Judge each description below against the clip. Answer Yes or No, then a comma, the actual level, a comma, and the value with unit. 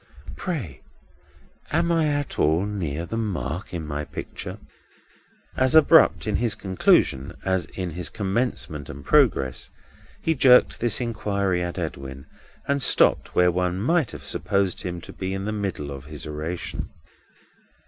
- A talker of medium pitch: No, very low, 95 Hz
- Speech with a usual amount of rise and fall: No, wide, 6.9 semitones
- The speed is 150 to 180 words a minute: No, average, 140 wpm